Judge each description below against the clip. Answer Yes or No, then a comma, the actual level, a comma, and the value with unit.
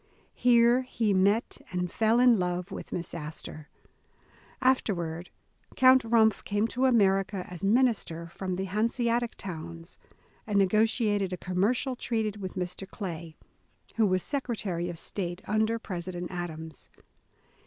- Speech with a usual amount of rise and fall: Yes, average, 4.4 semitones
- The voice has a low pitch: No, high, 195 Hz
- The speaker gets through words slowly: Yes, slow, 130 wpm